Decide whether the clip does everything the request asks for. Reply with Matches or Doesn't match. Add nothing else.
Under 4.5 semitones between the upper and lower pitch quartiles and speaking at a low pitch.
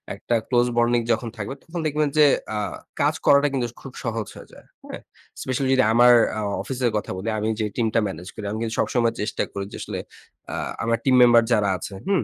Matches